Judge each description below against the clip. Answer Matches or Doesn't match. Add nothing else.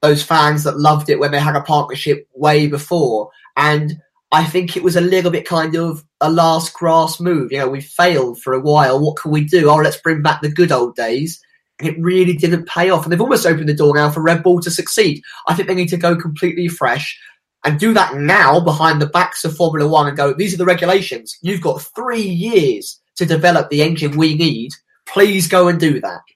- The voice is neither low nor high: Matches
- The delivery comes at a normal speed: Doesn't match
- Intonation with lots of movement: Doesn't match